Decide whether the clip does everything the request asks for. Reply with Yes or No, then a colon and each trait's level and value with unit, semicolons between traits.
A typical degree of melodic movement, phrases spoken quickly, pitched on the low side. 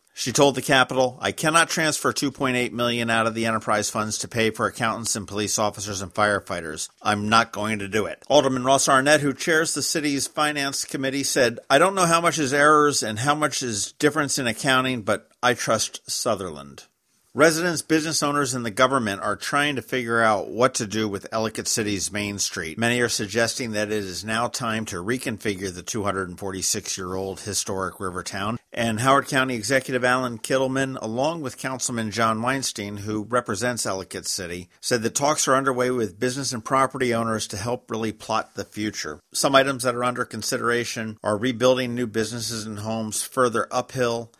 No: average, 3.9 semitones; average, 190 wpm; low, 120 Hz